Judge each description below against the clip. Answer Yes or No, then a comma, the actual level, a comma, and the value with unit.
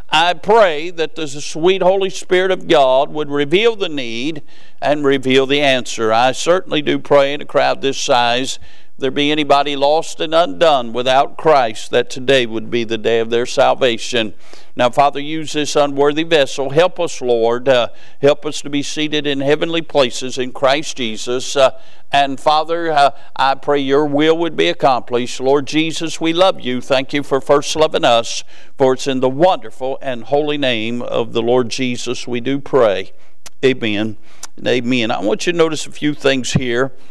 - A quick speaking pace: No, average, 180 wpm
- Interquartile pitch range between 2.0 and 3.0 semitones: No, average, 3.4 semitones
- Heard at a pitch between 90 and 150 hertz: Yes, medium, 140 Hz